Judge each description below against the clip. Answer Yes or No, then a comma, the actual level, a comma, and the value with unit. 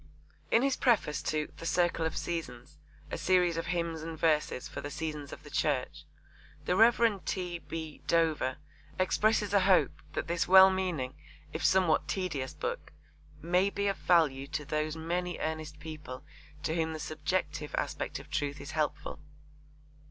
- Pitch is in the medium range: Yes, medium, 165 Hz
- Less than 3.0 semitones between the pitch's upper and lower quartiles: No, average, 3.4 semitones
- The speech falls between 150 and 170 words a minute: Yes, average, 160 wpm